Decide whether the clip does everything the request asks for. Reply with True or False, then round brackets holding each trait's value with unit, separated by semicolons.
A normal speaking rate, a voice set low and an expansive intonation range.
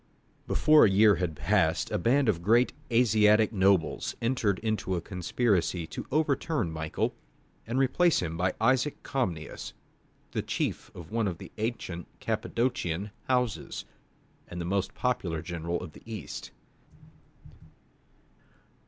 False (130 wpm; 105 Hz; 6.0 semitones)